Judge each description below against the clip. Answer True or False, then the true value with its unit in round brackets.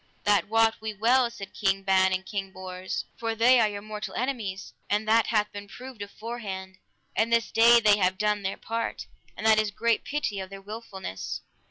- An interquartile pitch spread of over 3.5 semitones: False (2.8 semitones)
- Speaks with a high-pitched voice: True (210 Hz)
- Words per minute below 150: False (195 wpm)